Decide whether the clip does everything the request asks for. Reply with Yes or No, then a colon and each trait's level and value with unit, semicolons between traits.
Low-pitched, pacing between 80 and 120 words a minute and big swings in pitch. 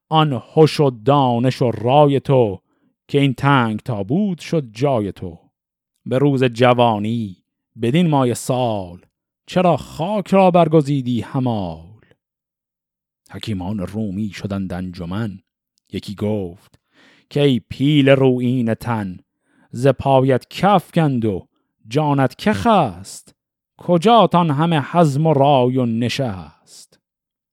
Yes: low, 125 Hz; average, 115 wpm; wide, 5.7 semitones